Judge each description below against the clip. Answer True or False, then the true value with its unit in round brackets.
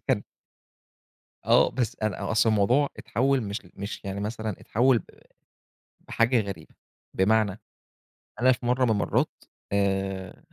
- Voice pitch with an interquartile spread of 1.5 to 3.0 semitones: False (3.4 semitones)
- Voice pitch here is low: True (110 Hz)